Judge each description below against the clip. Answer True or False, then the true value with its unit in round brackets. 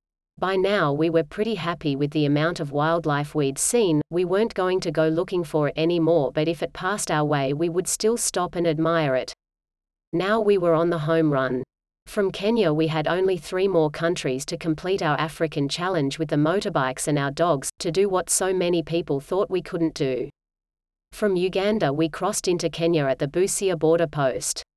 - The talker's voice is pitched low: False (165 Hz)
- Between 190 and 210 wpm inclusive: True (200 wpm)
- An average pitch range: True (3.2 semitones)